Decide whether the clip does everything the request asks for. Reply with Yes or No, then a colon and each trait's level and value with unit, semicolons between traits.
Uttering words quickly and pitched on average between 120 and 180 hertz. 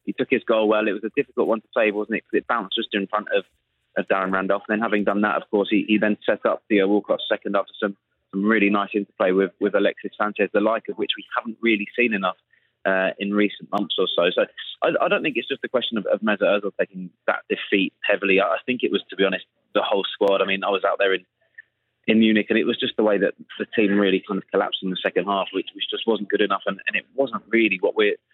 No: fast, 275 wpm; low, 105 Hz